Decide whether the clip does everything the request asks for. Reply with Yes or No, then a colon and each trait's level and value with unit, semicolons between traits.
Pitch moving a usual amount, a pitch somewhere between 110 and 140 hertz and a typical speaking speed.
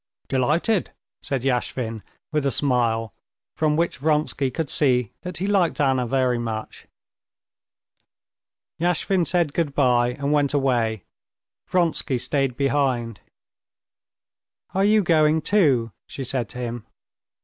No: average, 4.4 semitones; low, 135 Hz; slow, 120 wpm